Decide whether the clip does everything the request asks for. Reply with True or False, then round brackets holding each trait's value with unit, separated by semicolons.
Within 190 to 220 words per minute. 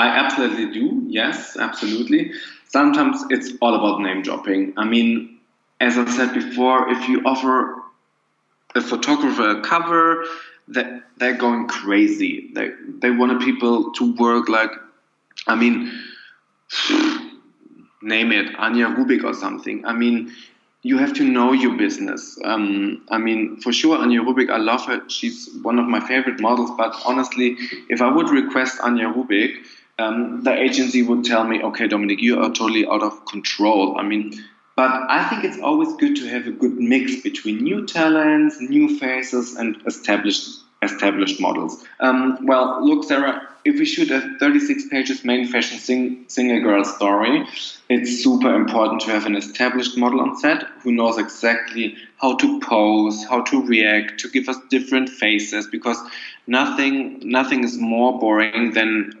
False (160 wpm)